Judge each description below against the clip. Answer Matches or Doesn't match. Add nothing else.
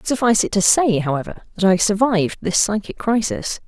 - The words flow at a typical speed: Matches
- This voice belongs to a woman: Matches